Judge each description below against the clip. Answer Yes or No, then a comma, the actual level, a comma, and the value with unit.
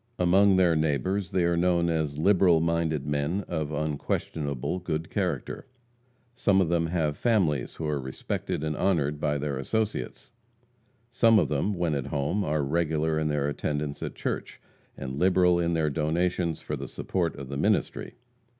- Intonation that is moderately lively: Yes, average, 3.5 semitones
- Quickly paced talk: No, average, 165 wpm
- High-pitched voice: No, very low, 80 Hz